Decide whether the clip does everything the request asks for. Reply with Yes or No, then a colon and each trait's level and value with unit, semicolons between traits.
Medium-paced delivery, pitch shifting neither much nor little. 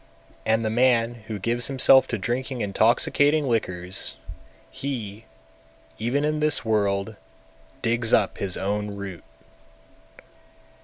No: slow, 110 wpm; average, 3.8 semitones